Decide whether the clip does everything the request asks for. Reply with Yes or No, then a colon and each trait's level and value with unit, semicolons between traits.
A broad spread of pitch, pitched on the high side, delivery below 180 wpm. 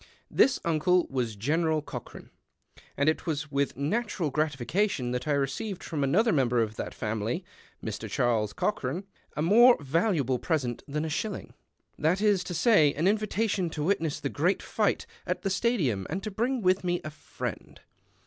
No: wide, 6.0 semitones; medium, 155 Hz; average, 170 wpm